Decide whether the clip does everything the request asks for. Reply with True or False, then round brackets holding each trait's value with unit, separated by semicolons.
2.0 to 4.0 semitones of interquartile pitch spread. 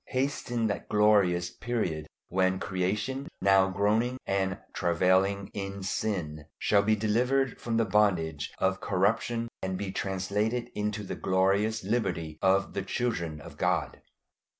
True (2.8 semitones)